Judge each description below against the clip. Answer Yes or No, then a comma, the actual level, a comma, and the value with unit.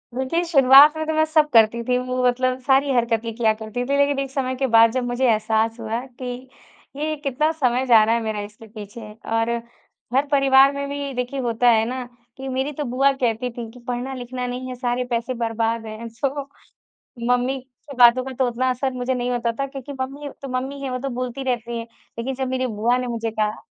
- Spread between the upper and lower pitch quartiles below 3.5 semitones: Yes, narrow, 2.6 semitones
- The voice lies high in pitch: Yes, very high, 250 Hz